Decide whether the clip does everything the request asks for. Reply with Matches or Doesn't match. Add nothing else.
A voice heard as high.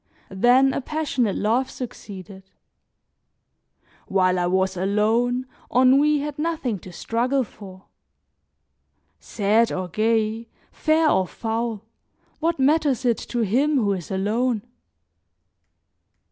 Matches